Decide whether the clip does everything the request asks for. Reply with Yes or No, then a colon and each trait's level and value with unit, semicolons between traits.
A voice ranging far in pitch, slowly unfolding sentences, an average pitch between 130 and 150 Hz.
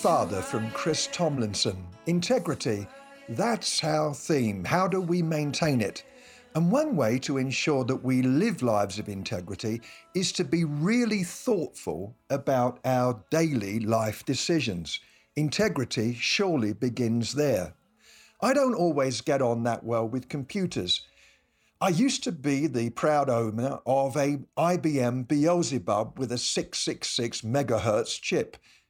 Yes: wide, 6.3 semitones; slow, 130 wpm; low, 135 Hz